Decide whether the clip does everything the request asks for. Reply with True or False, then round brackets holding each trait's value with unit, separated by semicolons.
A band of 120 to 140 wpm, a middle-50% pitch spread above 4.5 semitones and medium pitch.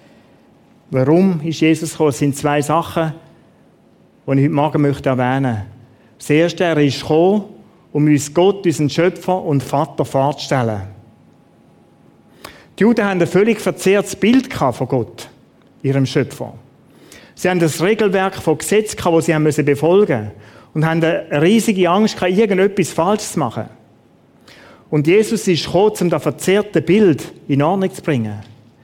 False (150 wpm; 5.2 semitones; 160 Hz)